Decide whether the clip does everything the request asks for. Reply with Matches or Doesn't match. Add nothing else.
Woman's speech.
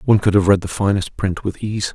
Doesn't match